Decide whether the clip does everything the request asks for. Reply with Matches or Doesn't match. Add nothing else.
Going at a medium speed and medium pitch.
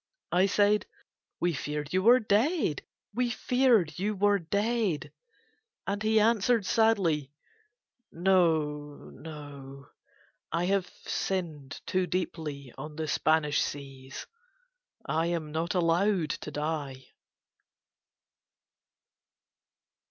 Doesn't match